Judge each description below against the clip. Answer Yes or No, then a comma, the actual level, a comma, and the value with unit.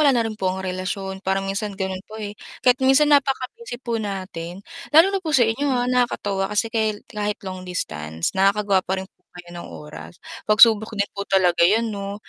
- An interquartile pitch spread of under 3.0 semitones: No, average, 3.7 semitones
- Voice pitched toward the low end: No, high, 200 Hz